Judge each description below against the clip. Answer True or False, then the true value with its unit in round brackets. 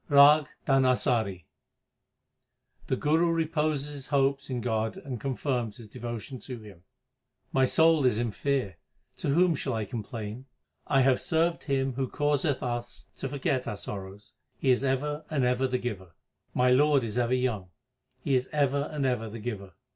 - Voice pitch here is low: True (130 Hz)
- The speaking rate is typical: True (165 wpm)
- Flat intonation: False (3.5 semitones)